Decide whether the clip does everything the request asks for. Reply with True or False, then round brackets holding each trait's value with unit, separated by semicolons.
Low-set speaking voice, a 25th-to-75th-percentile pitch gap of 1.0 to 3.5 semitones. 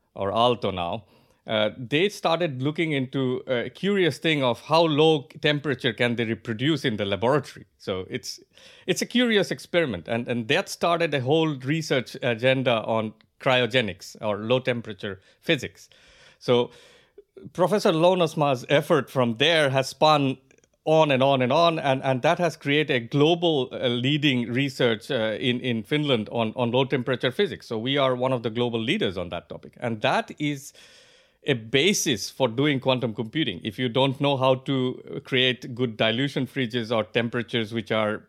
False (130 Hz; 4.3 semitones)